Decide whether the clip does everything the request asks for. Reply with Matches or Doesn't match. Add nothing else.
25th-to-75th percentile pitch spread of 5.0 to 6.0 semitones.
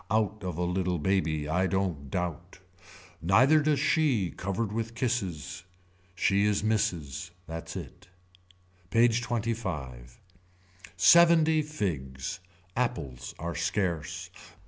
Matches